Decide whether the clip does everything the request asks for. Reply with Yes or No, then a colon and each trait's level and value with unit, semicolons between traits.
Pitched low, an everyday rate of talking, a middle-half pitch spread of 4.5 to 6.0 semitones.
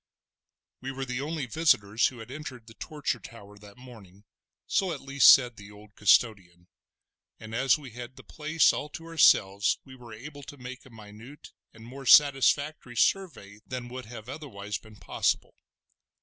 Yes: low, 125 Hz; average, 160 wpm; average, 4.8 semitones